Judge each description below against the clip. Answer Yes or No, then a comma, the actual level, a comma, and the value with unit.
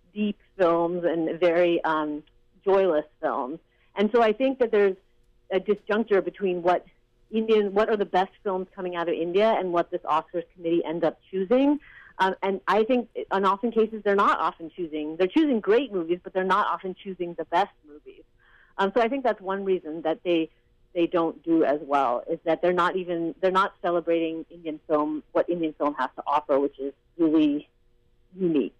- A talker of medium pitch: Yes, medium, 175 Hz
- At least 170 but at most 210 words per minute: Yes, average, 190 wpm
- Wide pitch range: No, average, 3.4 semitones